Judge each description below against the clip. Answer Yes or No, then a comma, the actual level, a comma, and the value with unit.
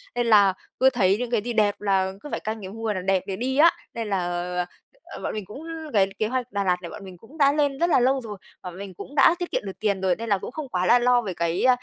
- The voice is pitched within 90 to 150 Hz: No, high, 215 Hz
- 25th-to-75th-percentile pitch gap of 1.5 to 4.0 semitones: No, average, 4.8 semitones